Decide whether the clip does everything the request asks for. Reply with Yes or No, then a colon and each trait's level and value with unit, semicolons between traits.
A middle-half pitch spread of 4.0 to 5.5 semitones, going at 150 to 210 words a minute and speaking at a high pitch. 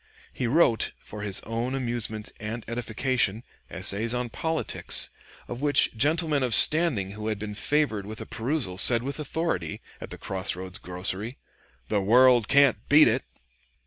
No: average, 4.4 semitones; average, 155 wpm; low, 115 Hz